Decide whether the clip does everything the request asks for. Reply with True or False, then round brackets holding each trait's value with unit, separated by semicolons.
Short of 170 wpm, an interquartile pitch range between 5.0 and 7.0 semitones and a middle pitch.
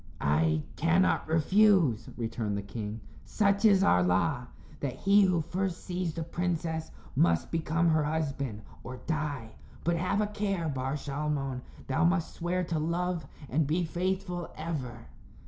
True (145 wpm; 5.3 semitones; 160 Hz)